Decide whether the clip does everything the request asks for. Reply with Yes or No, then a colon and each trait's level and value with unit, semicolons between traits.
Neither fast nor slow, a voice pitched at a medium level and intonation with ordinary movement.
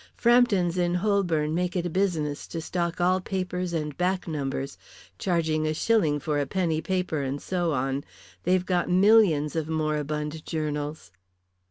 Yes: average, 155 wpm; medium, 165 Hz; average, 3.3 semitones